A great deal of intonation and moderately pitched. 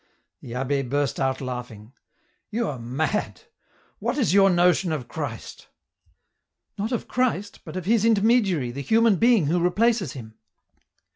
Yes: wide, 8.6 semitones; medium, 175 Hz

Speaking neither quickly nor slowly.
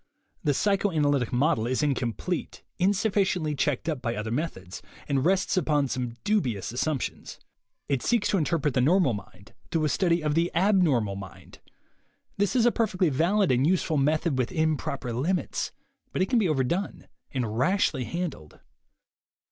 Yes: average, 155 wpm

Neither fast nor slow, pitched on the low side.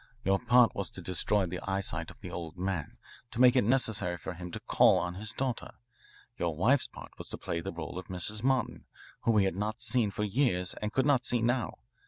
No: fast, 225 wpm; low, 100 Hz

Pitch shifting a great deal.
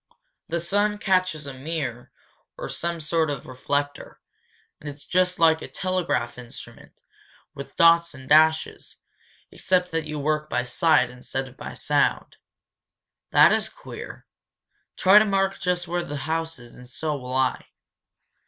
No: average, 4.5 semitones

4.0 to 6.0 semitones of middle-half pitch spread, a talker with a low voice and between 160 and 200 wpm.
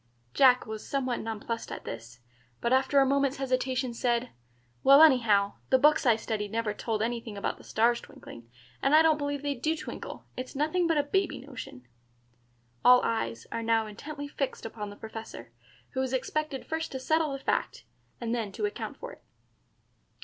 No: average, 4.3 semitones; very high, 255 Hz; average, 180 wpm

